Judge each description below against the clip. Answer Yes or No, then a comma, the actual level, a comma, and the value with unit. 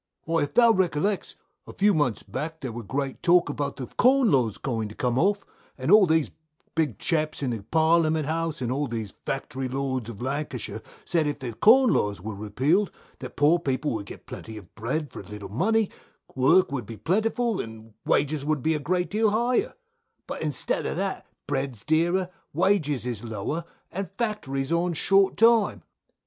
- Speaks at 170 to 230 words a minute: Yes, average, 185 wpm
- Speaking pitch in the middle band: Yes, medium, 150 Hz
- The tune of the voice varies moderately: No, wide, 6.3 semitones